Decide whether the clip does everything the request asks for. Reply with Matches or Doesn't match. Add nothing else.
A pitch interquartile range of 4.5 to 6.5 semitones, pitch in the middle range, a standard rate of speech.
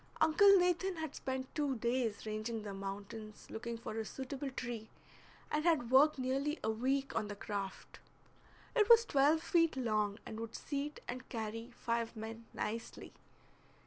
Doesn't match